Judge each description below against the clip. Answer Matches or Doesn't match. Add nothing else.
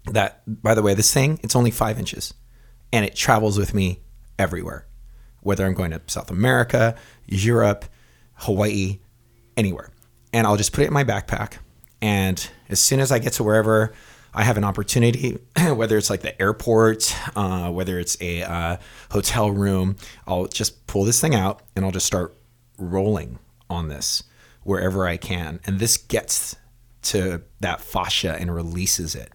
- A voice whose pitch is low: Matches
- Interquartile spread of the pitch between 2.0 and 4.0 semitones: Matches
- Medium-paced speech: Matches